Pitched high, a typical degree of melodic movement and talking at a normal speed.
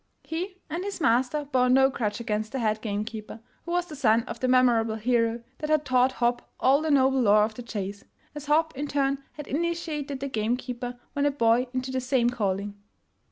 No: very high, 255 Hz; average, 4.0 semitones; fast, 210 wpm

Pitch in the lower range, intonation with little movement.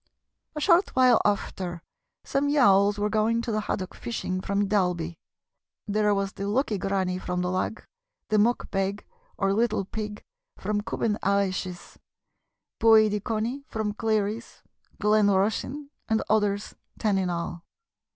No: high, 205 Hz; narrow, 2.2 semitones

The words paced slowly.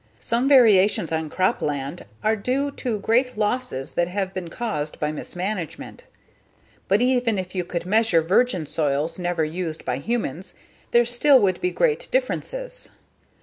No: average, 150 wpm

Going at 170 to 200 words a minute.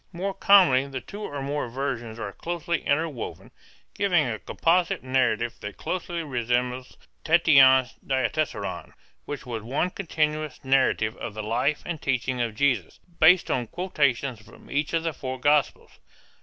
No: average, 145 wpm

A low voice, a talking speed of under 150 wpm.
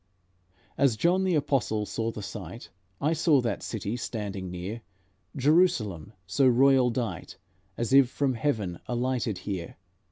Yes: low, 120 Hz; slow, 135 wpm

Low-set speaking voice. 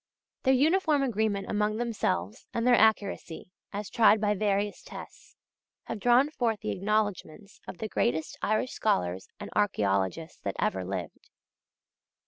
No: high, 210 Hz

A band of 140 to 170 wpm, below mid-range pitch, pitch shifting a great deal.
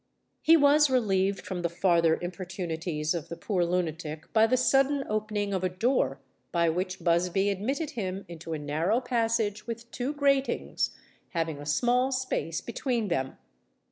No: average, 155 wpm; high, 195 Hz; wide, 6.2 semitones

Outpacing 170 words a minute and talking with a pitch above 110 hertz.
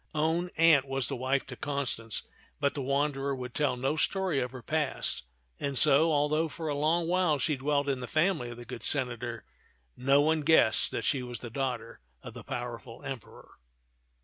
Yes: average, 190 wpm; medium, 140 Hz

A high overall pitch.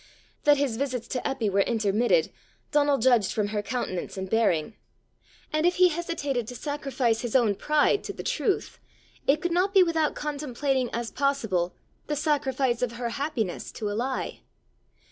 Yes: very high, 255 Hz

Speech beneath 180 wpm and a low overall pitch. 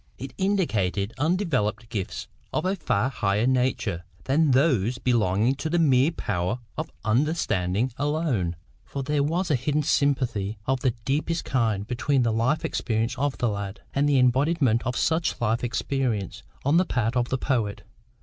Yes: average, 160 wpm; low, 125 Hz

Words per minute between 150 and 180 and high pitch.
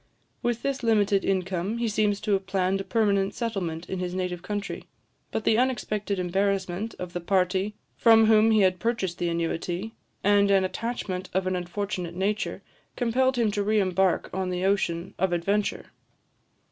Yes: average, 170 wpm; high, 195 Hz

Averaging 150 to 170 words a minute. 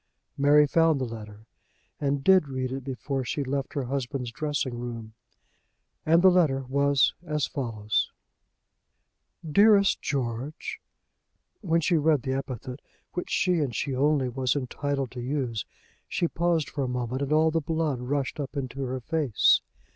Yes: average, 155 wpm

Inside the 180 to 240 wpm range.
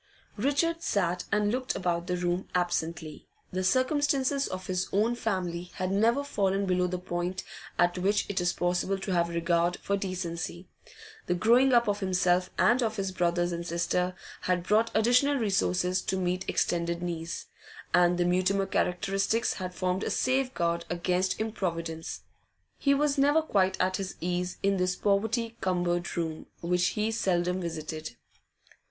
No: average, 155 wpm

